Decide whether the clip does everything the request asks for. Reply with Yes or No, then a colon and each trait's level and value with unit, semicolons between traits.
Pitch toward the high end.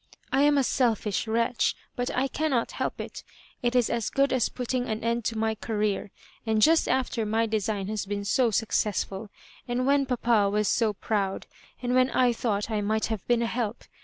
Yes: high, 230 Hz